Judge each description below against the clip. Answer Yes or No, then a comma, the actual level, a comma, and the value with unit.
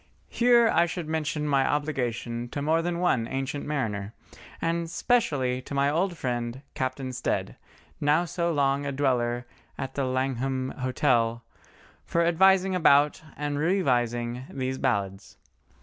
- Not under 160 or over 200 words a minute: No, slow, 135 wpm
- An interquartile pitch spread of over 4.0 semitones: Yes, average, 4.5 semitones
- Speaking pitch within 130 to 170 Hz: Yes, medium, 140 Hz